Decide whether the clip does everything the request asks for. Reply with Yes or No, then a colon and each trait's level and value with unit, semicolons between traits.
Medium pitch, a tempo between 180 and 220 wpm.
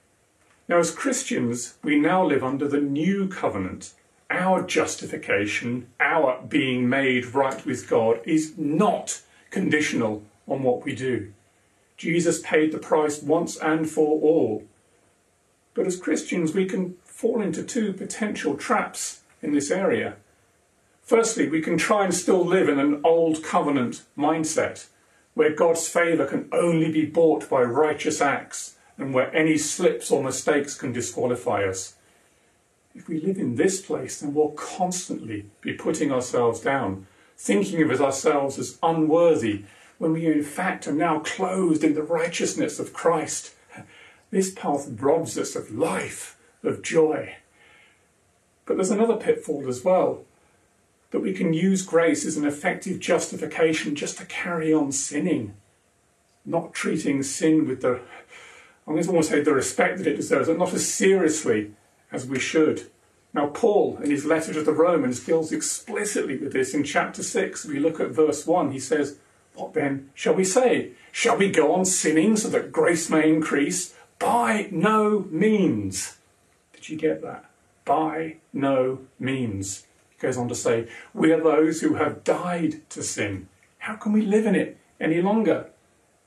No: medium, 155 Hz; average, 155 wpm